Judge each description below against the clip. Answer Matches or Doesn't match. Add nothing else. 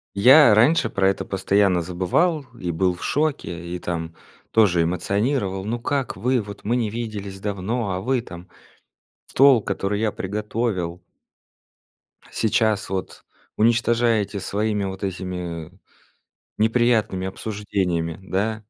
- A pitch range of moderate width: Matches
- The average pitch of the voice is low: Matches